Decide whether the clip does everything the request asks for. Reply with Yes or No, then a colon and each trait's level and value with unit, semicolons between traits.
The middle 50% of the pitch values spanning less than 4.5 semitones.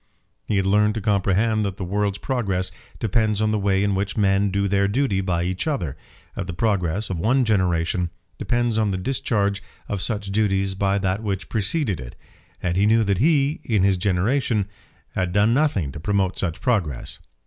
Yes: narrow, 2.5 semitones